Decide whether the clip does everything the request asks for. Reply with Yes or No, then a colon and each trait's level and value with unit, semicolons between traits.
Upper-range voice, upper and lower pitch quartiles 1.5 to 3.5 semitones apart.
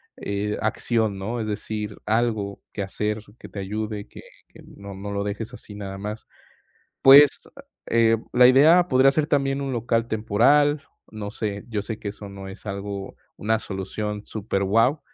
No: low, 105 Hz; average, 2.7 semitones